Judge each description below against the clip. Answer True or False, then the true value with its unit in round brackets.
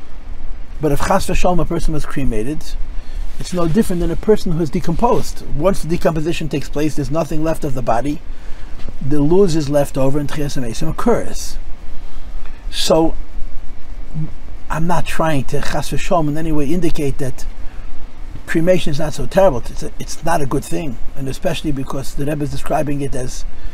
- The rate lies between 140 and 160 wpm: False (170 wpm)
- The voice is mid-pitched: True (150 Hz)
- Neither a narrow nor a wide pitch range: True (3.5 semitones)